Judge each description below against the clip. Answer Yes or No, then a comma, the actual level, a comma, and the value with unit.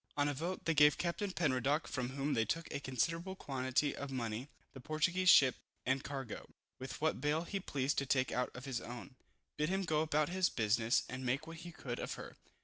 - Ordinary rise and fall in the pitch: Yes, average, 4.0 semitones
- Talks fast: Yes, fast, 215 wpm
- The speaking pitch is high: No, medium, 140 Hz